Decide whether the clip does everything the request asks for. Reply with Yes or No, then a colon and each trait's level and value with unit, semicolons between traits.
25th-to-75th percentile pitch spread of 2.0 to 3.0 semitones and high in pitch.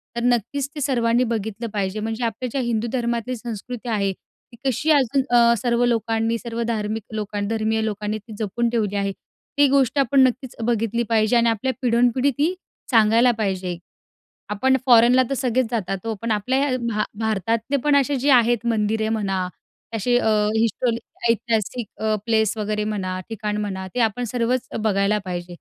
Yes: narrow, 2.6 semitones; high, 230 Hz